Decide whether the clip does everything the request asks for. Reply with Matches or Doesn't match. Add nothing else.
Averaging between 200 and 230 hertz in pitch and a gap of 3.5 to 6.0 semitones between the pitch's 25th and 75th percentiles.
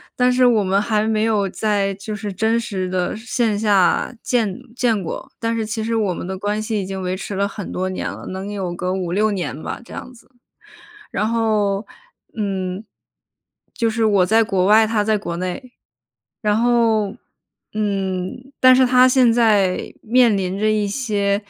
Doesn't match